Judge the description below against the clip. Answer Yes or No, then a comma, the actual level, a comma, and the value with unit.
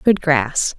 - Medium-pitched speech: Yes, medium, 170 Hz